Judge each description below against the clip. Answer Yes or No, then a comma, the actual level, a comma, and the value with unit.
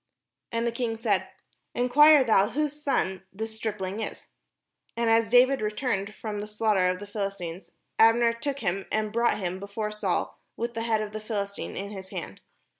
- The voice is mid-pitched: No, high, 215 Hz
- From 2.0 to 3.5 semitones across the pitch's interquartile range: Yes, narrow, 2.6 semitones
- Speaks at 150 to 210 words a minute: Yes, average, 185 wpm